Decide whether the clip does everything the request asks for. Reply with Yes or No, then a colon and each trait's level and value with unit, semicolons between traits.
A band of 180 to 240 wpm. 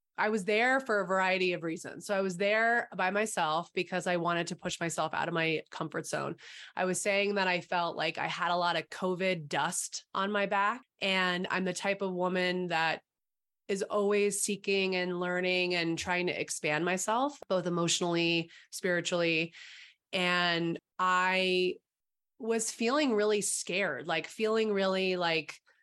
No: average, 165 wpm